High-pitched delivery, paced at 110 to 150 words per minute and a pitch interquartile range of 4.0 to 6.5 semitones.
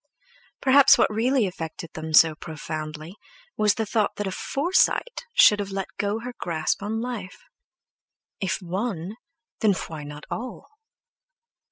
Yes: high, 200 Hz; average, 140 wpm; wide, 5.6 semitones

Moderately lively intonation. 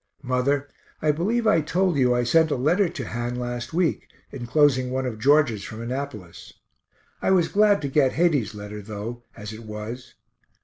Yes: average, 4.8 semitones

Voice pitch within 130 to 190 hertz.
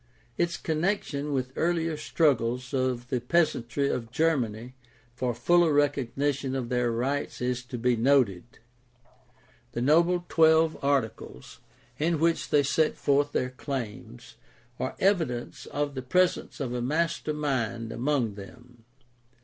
Yes: low, 135 Hz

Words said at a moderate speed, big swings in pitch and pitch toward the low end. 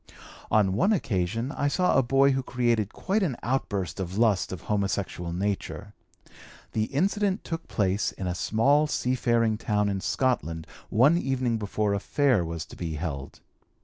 Yes: average, 160 wpm; wide, 5.8 semitones; low, 110 Hz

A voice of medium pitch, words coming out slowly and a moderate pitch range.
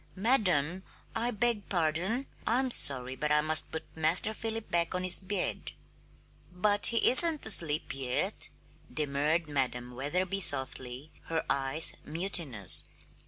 No: medium, 165 Hz; slow, 125 wpm; wide, 6.0 semitones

